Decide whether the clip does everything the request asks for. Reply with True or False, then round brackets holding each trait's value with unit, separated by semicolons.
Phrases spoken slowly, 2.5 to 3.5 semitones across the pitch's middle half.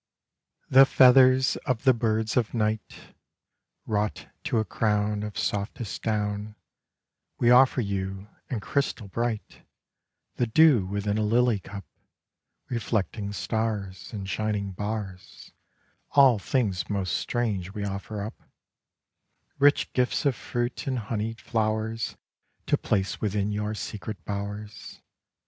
True (120 wpm; 2.8 semitones)